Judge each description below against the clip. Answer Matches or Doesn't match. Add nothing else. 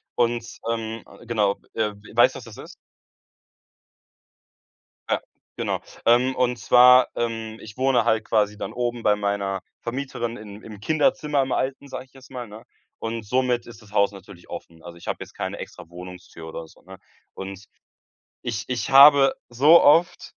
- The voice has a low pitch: Matches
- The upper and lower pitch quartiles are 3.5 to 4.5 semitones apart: Matches